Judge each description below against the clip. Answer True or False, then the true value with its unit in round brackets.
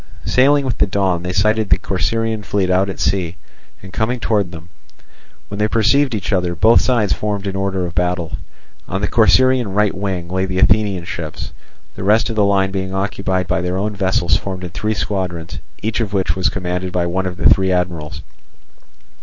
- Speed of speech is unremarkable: True (195 wpm)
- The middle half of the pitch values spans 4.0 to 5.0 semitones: False (2.7 semitones)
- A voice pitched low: True (95 Hz)